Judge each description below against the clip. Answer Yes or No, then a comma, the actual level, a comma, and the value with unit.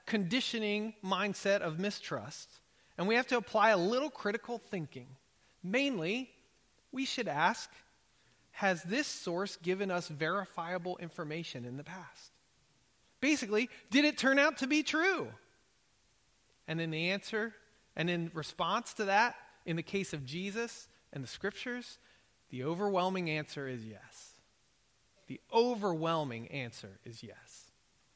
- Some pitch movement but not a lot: No, wide, 6.3 semitones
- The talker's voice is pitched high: Yes, high, 195 Hz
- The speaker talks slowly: Yes, slow, 130 wpm